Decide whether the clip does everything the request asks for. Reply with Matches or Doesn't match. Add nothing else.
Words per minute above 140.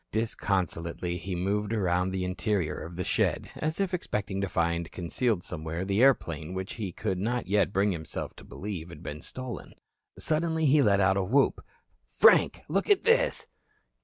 Matches